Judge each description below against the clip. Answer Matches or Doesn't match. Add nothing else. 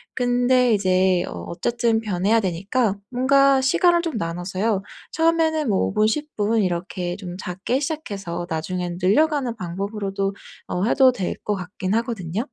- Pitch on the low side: Doesn't match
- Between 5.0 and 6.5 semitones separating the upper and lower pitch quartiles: Matches